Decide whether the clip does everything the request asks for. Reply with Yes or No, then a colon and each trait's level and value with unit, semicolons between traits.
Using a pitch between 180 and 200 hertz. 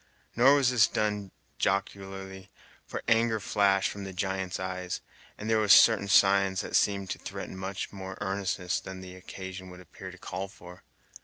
No: very low, 95 Hz